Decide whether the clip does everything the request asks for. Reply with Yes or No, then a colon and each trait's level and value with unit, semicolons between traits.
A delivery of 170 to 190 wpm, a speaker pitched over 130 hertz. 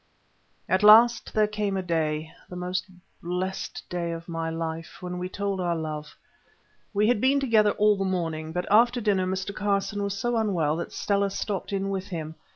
Yes: average, 175 wpm; high, 190 Hz